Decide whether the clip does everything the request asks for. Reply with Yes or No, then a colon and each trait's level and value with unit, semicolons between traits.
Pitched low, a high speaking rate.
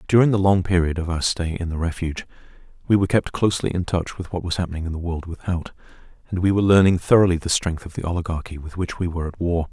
Yes: very low, 90 Hz; fast, 245 wpm